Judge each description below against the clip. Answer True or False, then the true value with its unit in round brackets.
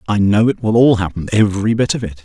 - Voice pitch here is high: False (105 Hz)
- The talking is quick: True (270 wpm)